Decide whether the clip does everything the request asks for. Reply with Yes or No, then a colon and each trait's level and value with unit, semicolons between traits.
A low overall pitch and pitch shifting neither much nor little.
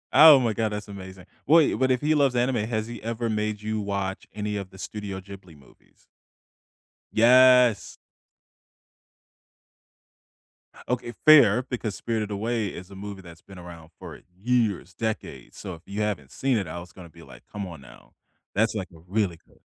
Yes: low, 105 Hz; average, 3.9 semitones